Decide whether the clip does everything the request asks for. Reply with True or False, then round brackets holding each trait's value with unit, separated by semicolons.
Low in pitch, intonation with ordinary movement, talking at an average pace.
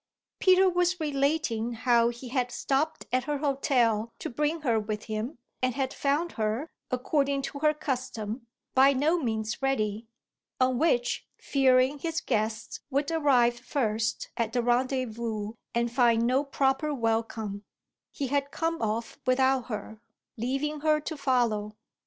False (255 Hz; 3.8 semitones; 145 wpm)